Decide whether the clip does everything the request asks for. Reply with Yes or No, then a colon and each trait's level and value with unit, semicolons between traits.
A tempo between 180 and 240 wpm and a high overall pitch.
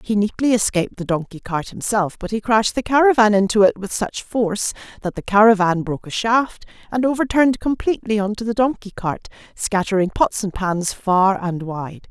Yes: average, 190 wpm; high, 210 Hz